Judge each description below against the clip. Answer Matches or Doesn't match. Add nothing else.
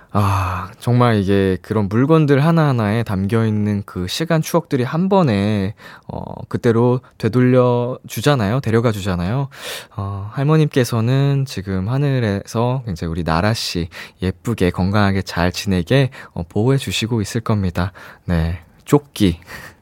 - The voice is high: Doesn't match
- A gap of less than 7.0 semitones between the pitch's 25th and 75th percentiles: Matches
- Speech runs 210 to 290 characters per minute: Matches